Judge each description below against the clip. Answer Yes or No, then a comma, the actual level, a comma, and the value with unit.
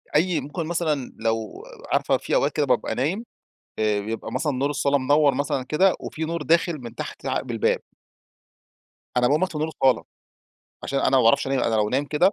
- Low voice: No, medium, 145 Hz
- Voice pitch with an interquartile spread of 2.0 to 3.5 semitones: No, average, 4.0 semitones